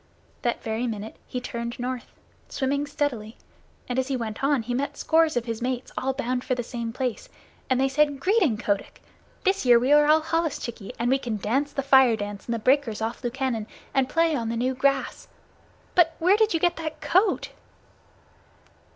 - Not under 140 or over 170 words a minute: No, average, 195 wpm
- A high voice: Yes, very high, 260 Hz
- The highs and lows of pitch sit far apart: No, average, 3.8 semitones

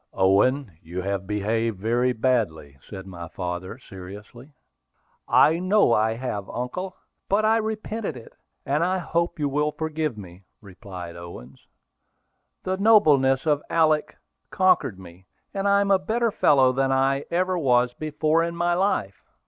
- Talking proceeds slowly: No, average, 150 wpm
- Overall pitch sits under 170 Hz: Yes, low, 135 Hz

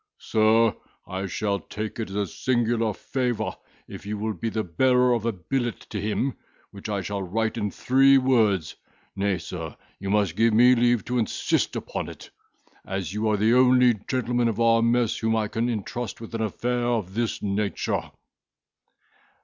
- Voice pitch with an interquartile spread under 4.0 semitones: Yes, average, 3.0 semitones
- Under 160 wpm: No, average, 175 wpm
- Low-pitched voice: Yes, low, 110 Hz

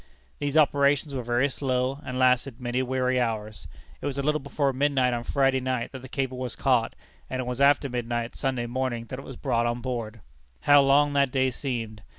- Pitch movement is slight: Yes, narrow, 2.2 semitones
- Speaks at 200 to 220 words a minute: Yes, fast, 205 wpm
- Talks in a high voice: No, low, 130 Hz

